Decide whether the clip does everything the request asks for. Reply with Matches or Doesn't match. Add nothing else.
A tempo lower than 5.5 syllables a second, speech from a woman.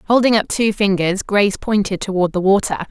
Doesn't match